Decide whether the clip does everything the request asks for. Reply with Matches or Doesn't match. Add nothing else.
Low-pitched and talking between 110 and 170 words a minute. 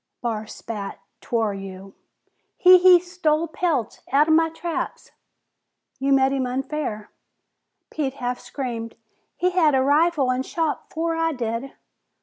Doesn't match